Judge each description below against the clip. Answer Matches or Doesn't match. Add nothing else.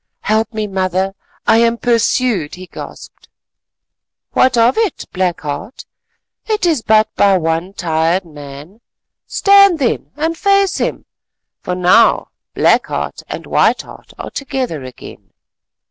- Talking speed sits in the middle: Doesn't match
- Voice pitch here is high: Matches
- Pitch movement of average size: Doesn't match